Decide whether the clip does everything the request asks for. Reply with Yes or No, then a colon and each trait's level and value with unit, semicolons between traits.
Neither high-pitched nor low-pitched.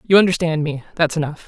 Yes: medium, 160 Hz